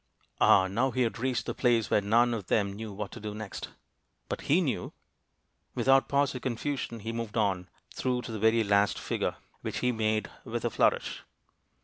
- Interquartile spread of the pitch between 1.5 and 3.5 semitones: Yes, average, 3.1 semitones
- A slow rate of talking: No, average, 195 wpm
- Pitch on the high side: No, low, 115 Hz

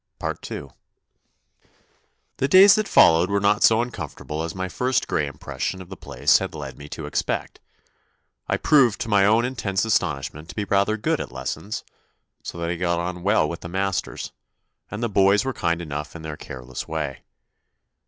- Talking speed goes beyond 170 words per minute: Yes, average, 185 wpm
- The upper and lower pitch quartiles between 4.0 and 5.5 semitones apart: Yes, average, 5.1 semitones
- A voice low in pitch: Yes, very low, 95 Hz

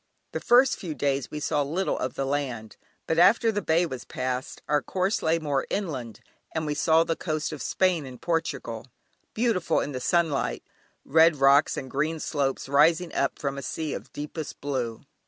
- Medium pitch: Yes, medium, 150 Hz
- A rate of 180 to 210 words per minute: Yes, average, 185 wpm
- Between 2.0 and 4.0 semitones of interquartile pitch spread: Yes, average, 3.3 semitones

